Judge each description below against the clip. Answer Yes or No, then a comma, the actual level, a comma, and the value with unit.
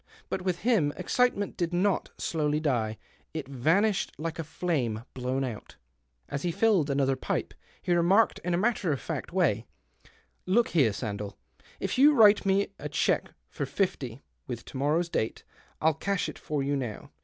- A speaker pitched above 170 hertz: No, medium, 160 Hz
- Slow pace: No, average, 180 wpm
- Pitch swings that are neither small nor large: No, wide, 6.2 semitones